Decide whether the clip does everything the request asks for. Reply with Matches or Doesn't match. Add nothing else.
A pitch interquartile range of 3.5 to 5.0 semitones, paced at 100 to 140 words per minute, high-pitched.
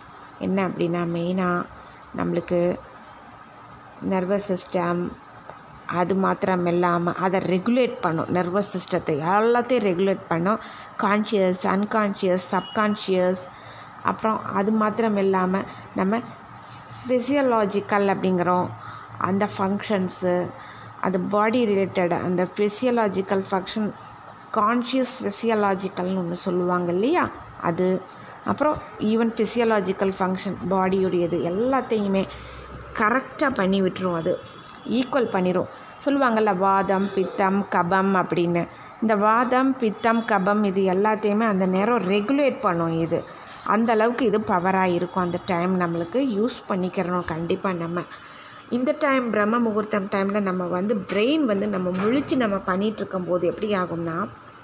Doesn't match